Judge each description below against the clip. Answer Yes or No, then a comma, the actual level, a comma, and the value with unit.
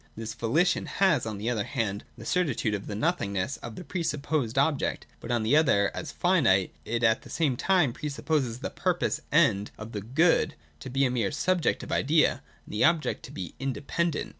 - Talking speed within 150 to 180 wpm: No, fast, 205 wpm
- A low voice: Yes, low, 130 Hz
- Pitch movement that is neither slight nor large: No, wide, 6.1 semitones